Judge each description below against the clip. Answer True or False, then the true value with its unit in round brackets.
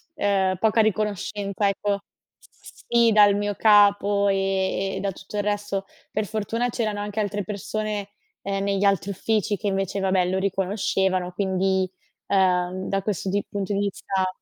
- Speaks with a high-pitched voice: True (200 Hz)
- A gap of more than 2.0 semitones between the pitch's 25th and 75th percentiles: False (1.3 semitones)